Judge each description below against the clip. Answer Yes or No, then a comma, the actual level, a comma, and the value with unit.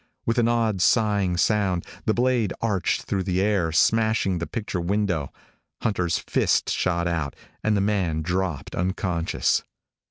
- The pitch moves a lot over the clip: No, average, 3.6 semitones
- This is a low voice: Yes, very low, 95 Hz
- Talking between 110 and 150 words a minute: Yes, average, 140 wpm